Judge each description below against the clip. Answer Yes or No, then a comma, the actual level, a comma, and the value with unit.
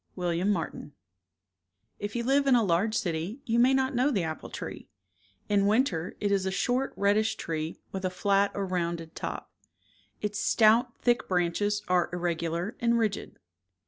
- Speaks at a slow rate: No, average, 165 wpm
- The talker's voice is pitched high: Yes, high, 200 Hz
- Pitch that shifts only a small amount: No, average, 4.8 semitones